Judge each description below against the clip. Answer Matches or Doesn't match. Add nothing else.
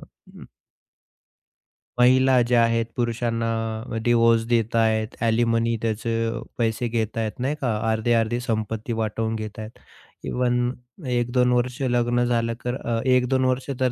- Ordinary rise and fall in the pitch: Doesn't match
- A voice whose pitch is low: Matches